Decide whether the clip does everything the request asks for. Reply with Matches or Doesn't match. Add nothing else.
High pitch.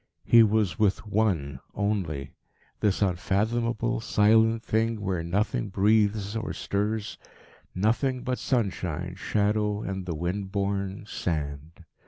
Doesn't match